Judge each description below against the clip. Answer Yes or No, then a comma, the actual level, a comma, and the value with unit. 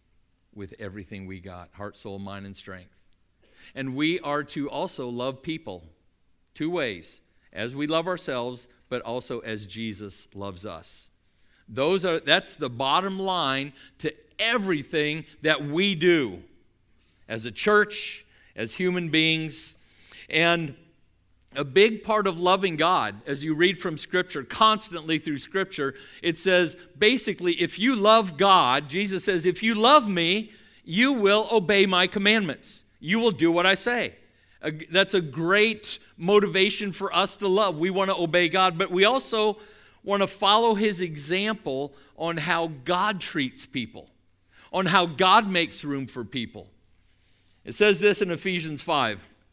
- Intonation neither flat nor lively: No, wide, 8.0 semitones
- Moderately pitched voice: Yes, medium, 165 Hz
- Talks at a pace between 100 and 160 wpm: Yes, average, 150 wpm